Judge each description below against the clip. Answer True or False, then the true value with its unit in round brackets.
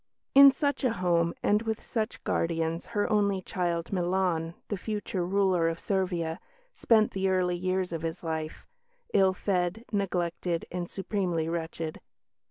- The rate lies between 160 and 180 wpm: False (145 wpm)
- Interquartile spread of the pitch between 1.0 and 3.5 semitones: True (3.2 semitones)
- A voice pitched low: False (180 Hz)